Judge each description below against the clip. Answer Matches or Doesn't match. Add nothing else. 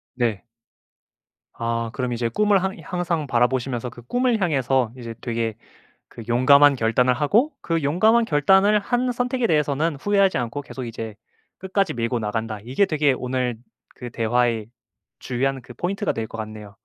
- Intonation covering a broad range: Matches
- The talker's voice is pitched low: Matches